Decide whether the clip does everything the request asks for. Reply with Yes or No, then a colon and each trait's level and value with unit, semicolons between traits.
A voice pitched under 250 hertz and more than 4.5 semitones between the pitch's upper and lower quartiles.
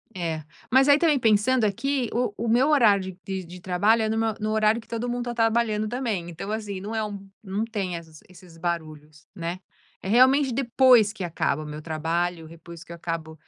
Yes: high, 205 Hz; average, 5.3 semitones